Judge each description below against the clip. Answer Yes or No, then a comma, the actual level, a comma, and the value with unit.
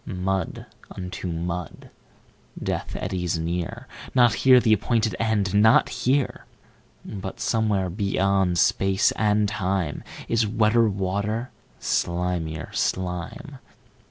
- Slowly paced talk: Yes, slow, 95 wpm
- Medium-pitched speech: No, low, 100 Hz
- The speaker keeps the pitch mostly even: No, average, 3.5 semitones